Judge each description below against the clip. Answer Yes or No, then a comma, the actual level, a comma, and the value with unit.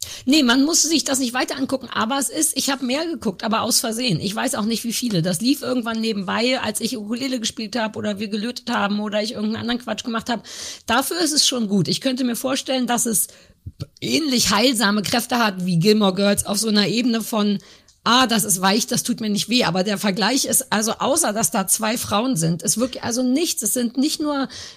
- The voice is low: No, high, 235 Hz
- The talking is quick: Yes, fast, 230 wpm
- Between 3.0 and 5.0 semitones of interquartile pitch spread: Yes, average, 3.6 semitones